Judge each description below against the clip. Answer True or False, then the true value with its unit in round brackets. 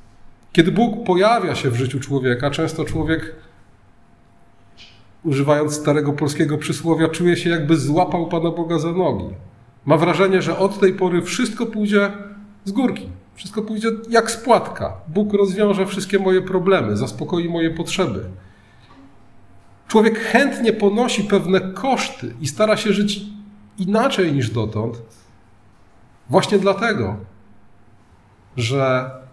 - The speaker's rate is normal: True (120 wpm)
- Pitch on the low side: False (165 Hz)